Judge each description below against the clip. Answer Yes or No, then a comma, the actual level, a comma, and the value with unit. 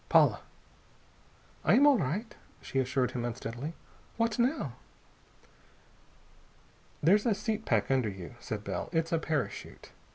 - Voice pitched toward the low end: No, medium, 155 Hz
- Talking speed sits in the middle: No, slow, 130 wpm